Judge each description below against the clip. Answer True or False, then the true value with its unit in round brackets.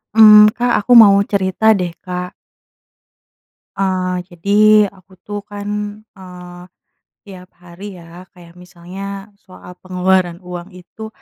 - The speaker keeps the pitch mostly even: True (2.1 semitones)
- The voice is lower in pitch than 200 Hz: True (185 Hz)